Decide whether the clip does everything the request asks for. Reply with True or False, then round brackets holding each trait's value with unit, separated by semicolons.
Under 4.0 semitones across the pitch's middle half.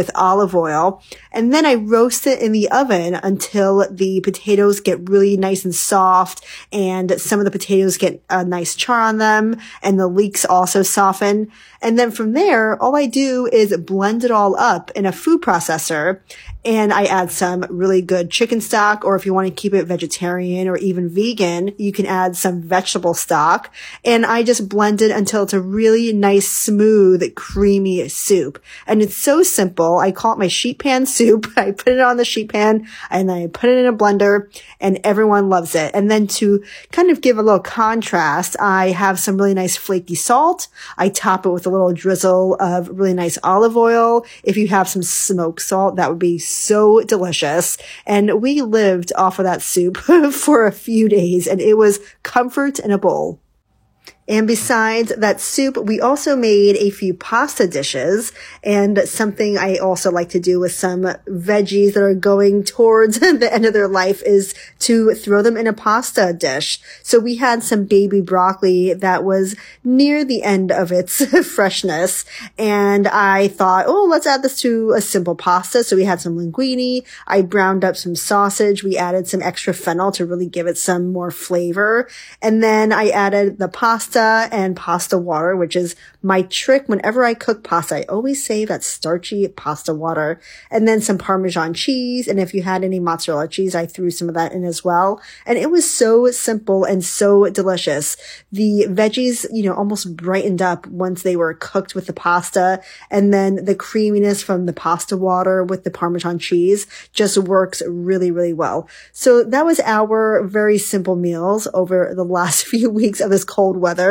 True (3.0 semitones)